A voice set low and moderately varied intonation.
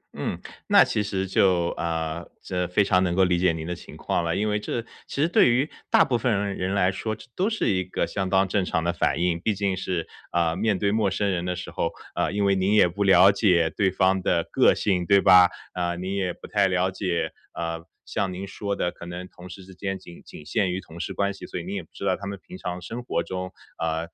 No: very low, 95 Hz; narrow, 2.2 semitones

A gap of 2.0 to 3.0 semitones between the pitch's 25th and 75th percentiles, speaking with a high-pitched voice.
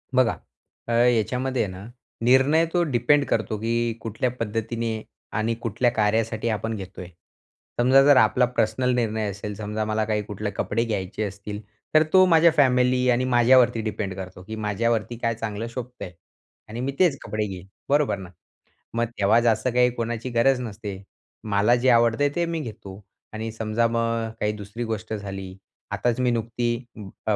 No: narrow, 2.6 semitones; low, 115 Hz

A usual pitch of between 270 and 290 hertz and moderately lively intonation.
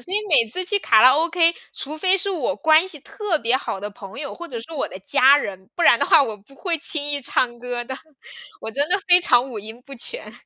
No: very high, 280 Hz; wide, 6.1 semitones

